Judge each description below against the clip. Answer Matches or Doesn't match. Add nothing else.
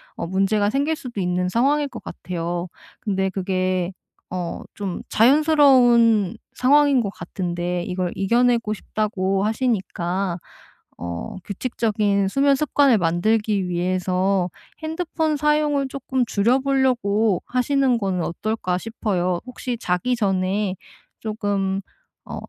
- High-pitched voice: Matches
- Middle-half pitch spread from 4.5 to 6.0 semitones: Matches